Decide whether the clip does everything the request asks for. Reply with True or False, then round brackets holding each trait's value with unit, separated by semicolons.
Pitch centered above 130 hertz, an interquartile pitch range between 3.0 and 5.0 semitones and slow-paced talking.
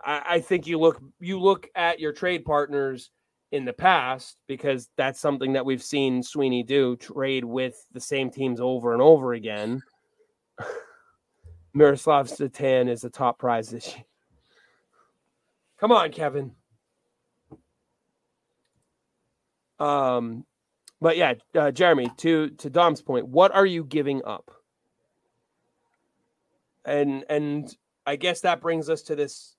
True (140 Hz; 4.6 semitones; 130 wpm)